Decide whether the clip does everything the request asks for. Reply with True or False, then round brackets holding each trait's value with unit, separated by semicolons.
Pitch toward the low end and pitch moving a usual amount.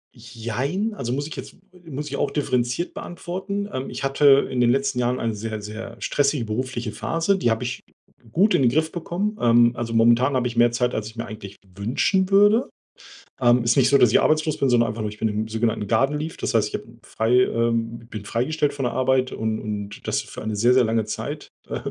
True (120 Hz; 4.0 semitones)